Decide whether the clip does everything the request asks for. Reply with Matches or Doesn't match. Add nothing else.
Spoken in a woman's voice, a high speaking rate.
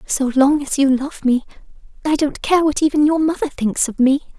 Matches